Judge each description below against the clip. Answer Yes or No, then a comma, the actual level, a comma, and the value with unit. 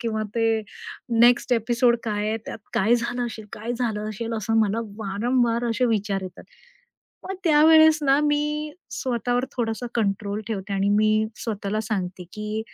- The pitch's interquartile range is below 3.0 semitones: Yes, narrow, 2.5 semitones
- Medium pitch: No, high, 225 Hz